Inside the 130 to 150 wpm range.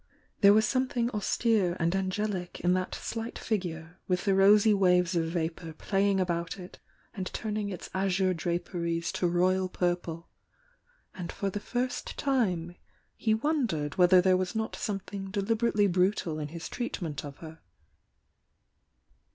Yes: average, 145 wpm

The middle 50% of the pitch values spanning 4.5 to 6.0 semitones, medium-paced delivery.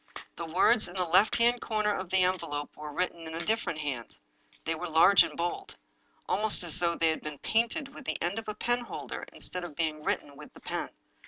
No: average, 5.1 semitones; fast, 220 wpm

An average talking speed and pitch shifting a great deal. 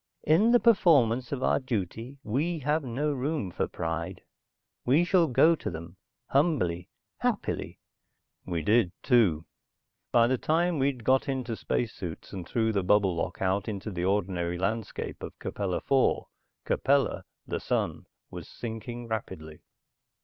Yes: average, 145 wpm; wide, 6.8 semitones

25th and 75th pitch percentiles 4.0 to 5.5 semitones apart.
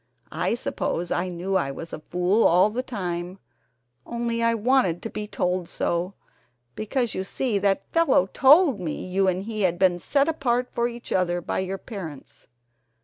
Yes: average, 5.0 semitones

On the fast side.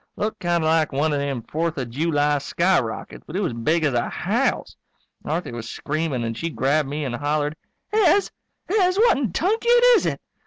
No: average, 195 wpm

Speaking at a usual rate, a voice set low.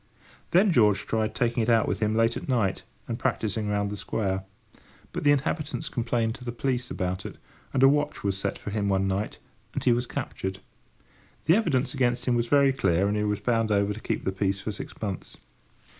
No: fast, 215 wpm; low, 110 Hz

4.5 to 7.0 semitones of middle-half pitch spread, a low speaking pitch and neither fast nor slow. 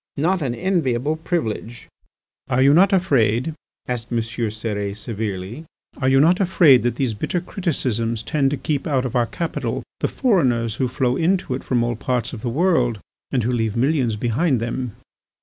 Yes: average, 5.2 semitones; low, 125 Hz; average, 175 wpm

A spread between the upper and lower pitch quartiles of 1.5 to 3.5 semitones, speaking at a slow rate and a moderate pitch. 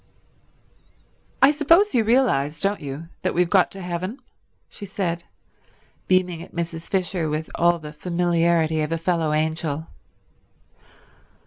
Yes: average, 3.0 semitones; slow, 130 wpm; medium, 170 Hz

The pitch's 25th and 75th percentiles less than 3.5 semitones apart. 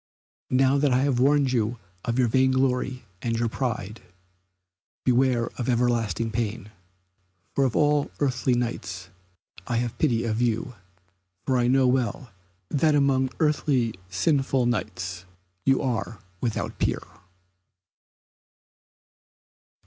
Yes: narrow, 2.4 semitones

